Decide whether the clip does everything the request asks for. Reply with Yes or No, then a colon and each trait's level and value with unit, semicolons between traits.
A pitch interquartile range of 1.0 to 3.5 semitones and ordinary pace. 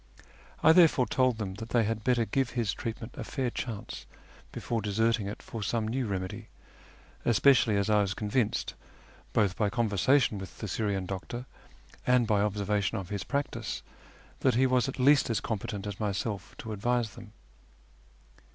Yes: average, 3.1 semitones; average, 170 wpm